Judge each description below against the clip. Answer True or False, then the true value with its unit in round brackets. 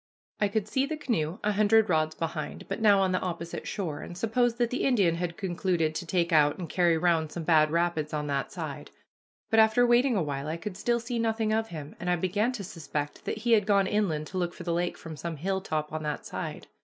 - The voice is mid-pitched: True (180 Hz)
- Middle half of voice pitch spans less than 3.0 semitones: False (5.2 semitones)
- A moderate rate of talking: False (240 wpm)